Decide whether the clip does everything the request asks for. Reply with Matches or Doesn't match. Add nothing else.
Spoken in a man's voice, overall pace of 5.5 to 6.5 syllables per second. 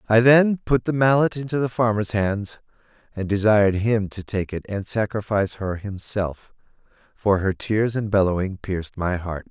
Doesn't match